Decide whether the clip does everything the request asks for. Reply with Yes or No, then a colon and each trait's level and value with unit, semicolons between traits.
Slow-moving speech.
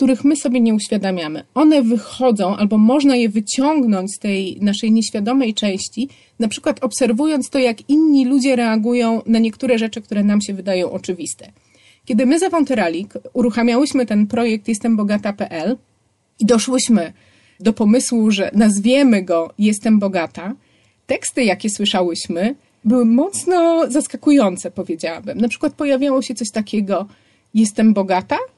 No: average, 135 wpm